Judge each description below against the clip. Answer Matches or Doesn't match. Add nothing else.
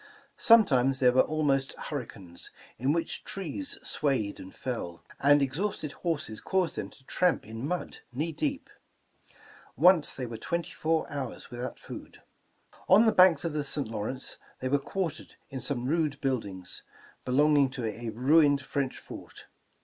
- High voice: Doesn't match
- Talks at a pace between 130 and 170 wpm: Matches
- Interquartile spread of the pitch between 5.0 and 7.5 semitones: Doesn't match